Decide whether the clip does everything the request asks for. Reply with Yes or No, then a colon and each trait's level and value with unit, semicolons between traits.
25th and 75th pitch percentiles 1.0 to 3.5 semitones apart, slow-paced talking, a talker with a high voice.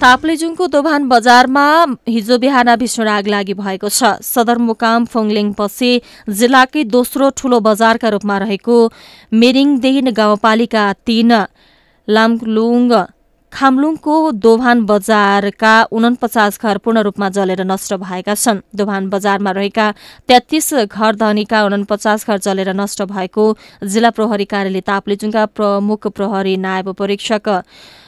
Yes: average, 2.9 semitones; slow, 115 wpm; high, 220 Hz